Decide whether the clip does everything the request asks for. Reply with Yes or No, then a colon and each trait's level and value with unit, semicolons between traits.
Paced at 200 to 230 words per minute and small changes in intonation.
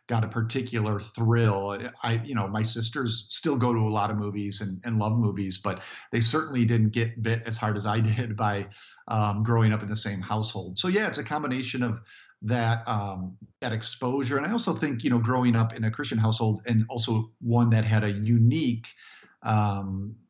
Yes: fast, 205 wpm; narrow, 2.1 semitones